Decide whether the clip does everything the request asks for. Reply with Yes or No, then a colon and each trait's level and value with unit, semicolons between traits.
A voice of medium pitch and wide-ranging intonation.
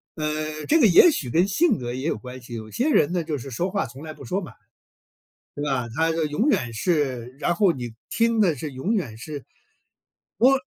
Yes: medium, 155 Hz; wide, 6.6 semitones